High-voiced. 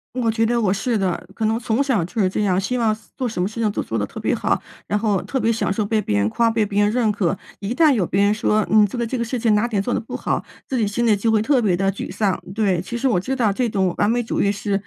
Yes: high, 215 Hz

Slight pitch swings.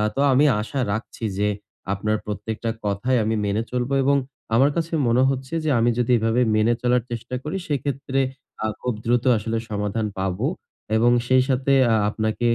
No: average, 3.1 semitones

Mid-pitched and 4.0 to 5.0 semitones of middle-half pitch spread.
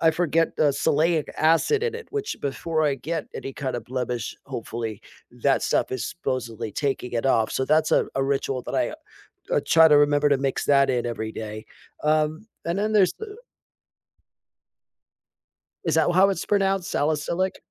Yes: medium, 145 Hz; average, 4.7 semitones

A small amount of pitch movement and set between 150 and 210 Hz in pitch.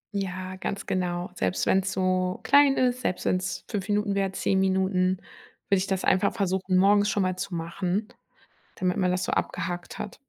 Yes: narrow, 1.4 semitones; medium, 185 Hz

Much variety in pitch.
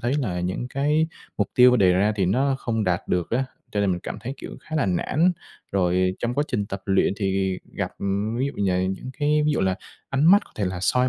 Yes: wide, 6.0 semitones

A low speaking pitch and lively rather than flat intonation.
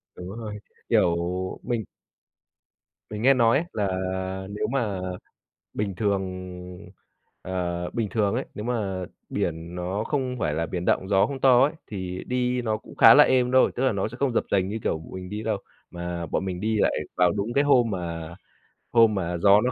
No: low, 105 Hz; average, 4.7 semitones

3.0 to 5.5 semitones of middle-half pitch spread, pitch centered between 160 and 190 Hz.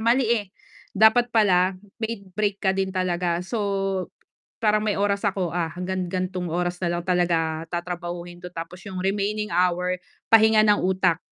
No: narrow, 2.6 semitones; medium, 185 Hz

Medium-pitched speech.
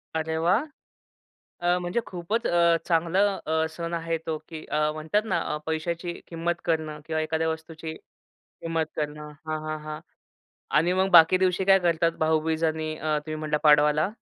Yes: medium, 160 Hz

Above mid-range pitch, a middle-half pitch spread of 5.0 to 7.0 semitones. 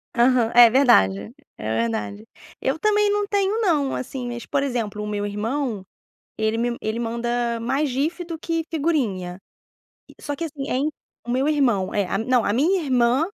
Yes: high, 245 Hz; average, 5.3 semitones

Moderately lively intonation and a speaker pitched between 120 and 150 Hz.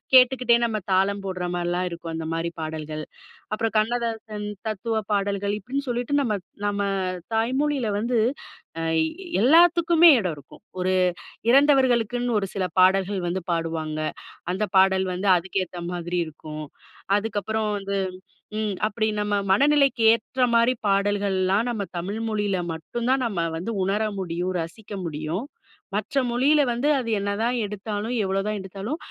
No: average, 4.1 semitones; high, 205 Hz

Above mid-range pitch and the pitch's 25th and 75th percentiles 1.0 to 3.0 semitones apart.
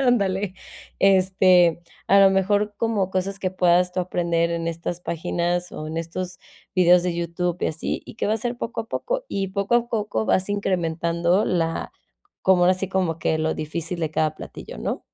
No: medium, 180 Hz; narrow, 2.6 semitones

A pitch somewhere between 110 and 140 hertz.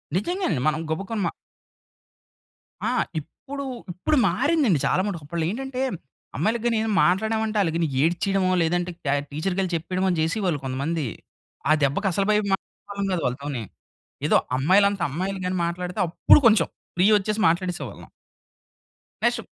No: medium, 185 Hz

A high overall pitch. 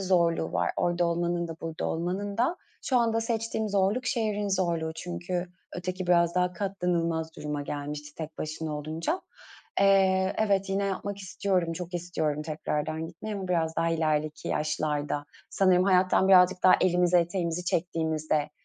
No: medium, 175 Hz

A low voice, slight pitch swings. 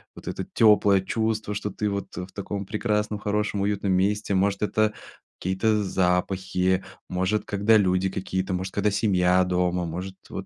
Yes: low, 100 Hz; narrow, 2.2 semitones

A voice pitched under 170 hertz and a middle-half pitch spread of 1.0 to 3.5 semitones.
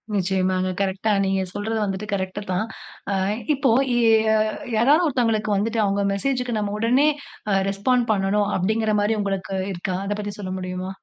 No: high, 205 Hz; average, 2.8 semitones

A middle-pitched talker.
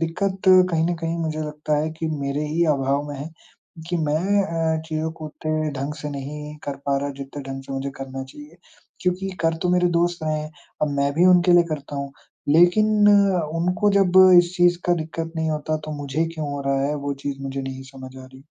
Yes: medium, 155 Hz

